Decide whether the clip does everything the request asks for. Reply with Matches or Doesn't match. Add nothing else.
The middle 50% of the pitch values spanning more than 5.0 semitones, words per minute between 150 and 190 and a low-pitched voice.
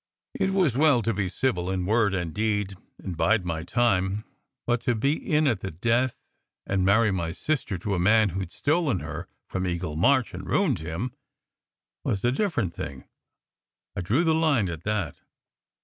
Matches